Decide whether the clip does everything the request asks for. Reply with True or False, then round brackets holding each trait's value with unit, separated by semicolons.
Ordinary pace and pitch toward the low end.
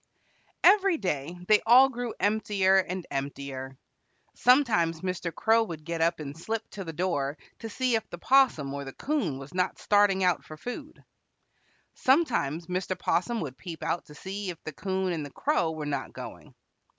False (175 wpm; 180 Hz)